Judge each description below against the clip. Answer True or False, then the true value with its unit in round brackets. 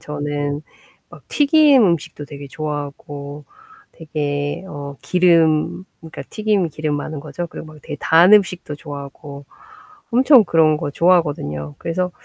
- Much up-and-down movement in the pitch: False (3.6 semitones)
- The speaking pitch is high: False (155 Hz)